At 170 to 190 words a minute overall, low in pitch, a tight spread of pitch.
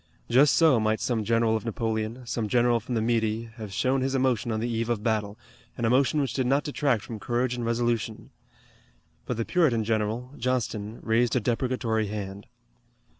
Yes: average, 180 wpm; low, 115 Hz; narrow, 2.3 semitones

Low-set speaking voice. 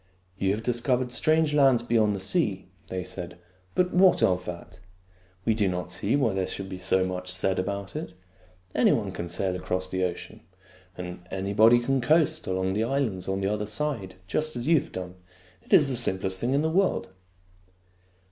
Yes: low, 100 Hz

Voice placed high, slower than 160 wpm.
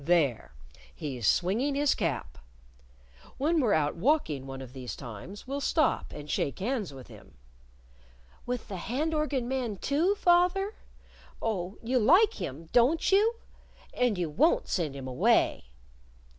Yes: high, 215 Hz; average, 145 wpm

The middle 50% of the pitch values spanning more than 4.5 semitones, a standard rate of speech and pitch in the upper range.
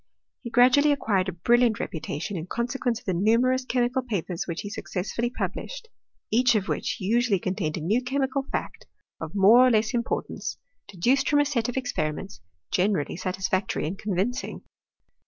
Yes: average, 5.0 semitones; average, 165 wpm; high, 220 Hz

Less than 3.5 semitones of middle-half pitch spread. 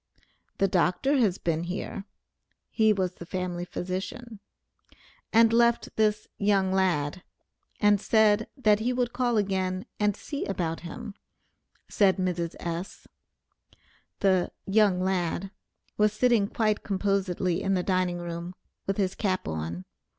Yes: average, 2.9 semitones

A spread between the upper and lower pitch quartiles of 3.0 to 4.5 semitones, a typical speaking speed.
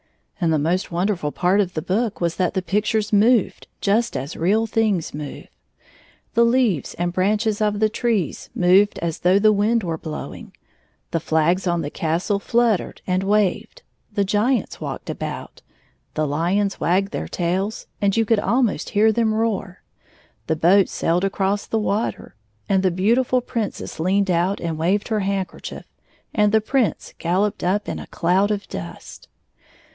Yes: average, 3.6 semitones; average, 165 wpm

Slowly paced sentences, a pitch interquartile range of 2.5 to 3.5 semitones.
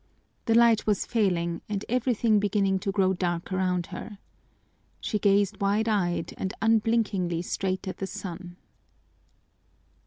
Yes: slow, 130 wpm; average, 2.8 semitones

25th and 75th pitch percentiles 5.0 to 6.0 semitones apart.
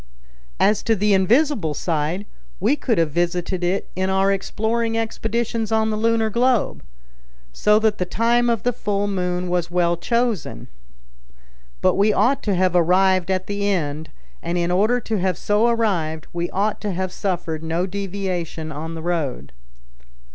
No: average, 3.9 semitones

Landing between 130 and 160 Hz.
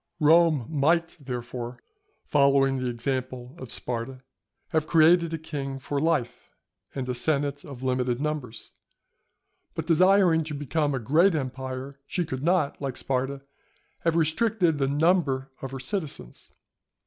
Yes: medium, 140 Hz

